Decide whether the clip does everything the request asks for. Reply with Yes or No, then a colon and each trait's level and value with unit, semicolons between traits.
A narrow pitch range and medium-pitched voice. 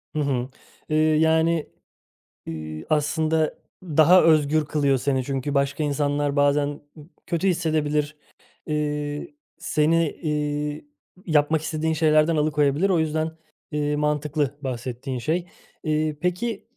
Yes: narrow, 1.7 semitones; medium, 150 Hz